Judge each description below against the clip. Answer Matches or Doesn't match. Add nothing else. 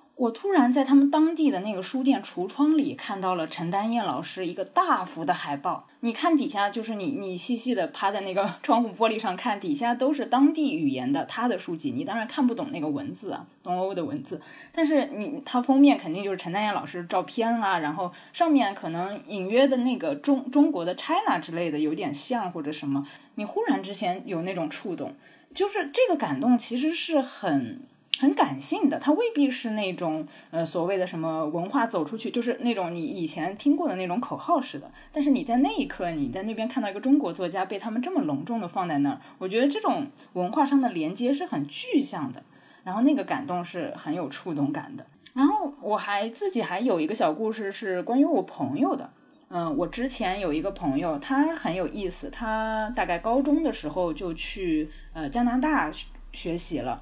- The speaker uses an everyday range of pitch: Doesn't match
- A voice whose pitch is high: Matches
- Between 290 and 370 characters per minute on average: Matches